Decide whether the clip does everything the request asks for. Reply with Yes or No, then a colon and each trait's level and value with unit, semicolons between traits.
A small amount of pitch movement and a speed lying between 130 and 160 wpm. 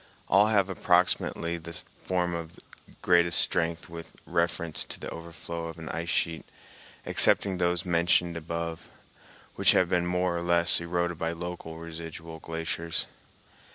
Yes: narrow, 1.0 semitones; average, 140 wpm